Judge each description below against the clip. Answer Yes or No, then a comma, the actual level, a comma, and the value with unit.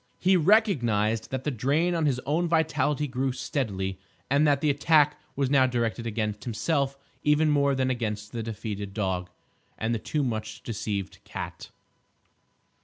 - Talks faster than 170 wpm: No, average, 155 wpm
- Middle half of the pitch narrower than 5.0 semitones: No, average, 5.3 semitones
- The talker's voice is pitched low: Yes, low, 130 Hz